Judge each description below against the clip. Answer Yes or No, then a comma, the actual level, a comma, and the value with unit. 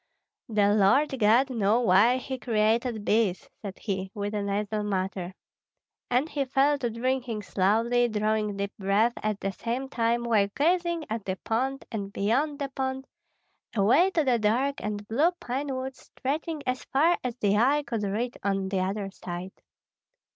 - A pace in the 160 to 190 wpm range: Yes, average, 165 wpm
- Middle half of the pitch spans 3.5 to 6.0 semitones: Yes, average, 4.5 semitones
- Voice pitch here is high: Yes, high, 230 Hz